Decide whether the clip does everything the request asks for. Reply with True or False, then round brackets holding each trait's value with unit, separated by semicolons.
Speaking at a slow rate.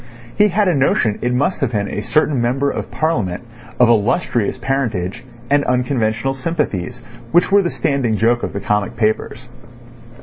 False (165 wpm)